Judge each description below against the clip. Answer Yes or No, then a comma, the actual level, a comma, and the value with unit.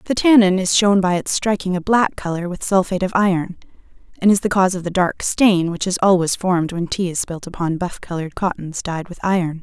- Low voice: No, medium, 185 Hz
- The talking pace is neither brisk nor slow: No, fast, 230 wpm